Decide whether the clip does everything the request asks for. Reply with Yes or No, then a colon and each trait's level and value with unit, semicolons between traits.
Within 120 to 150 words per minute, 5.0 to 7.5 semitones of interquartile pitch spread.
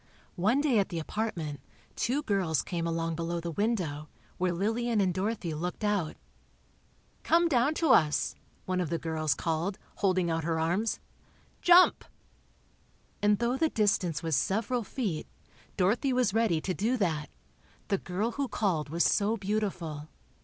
Yes: average, 145 wpm; average, 5.3 semitones